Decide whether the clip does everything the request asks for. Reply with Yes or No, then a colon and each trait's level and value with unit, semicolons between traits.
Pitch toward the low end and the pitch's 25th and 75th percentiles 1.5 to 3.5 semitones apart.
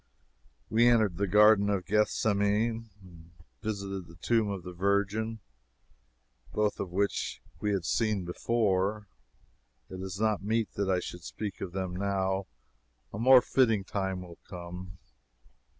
Yes: low, 100 Hz; narrow, 2.6 semitones